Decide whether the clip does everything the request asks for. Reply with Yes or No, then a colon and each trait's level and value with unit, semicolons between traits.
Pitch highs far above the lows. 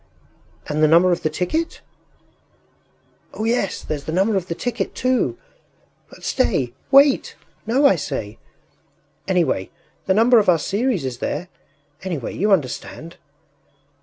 Yes: wide, 6.8 semitones